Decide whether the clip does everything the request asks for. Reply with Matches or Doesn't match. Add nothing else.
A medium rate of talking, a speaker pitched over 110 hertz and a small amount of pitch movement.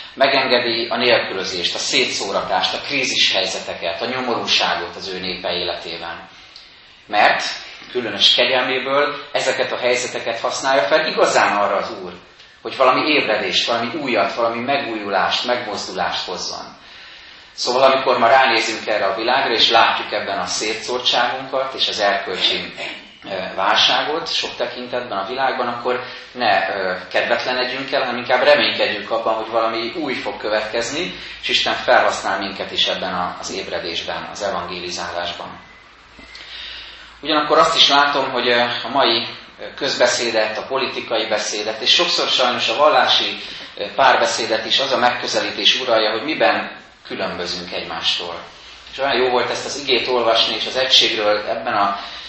Doesn't match